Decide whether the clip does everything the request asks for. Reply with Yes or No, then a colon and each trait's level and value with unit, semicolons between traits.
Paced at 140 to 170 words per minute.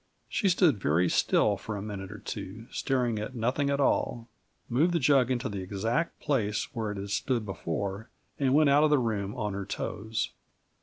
No: average, 195 wpm